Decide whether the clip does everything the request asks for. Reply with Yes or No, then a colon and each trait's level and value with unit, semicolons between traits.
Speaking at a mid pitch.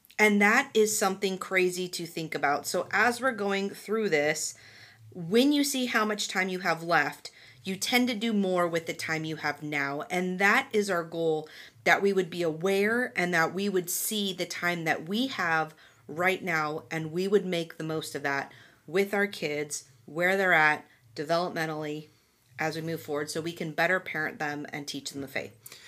Yes: medium, 170 Hz